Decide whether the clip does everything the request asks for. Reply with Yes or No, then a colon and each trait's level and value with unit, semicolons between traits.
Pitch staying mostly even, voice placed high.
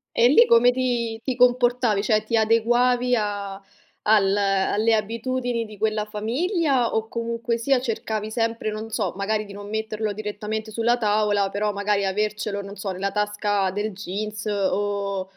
Yes: narrow, 2.2 semitones; high, 215 Hz